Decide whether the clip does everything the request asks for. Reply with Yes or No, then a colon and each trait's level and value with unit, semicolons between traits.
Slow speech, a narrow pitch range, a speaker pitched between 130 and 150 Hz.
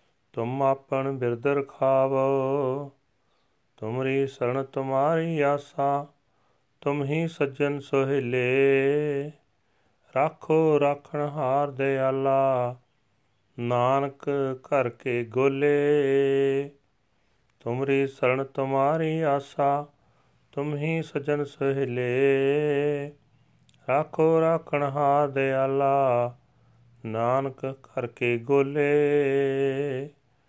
Yes: slow, 65 wpm; narrow, 1.6 semitones; low, 135 Hz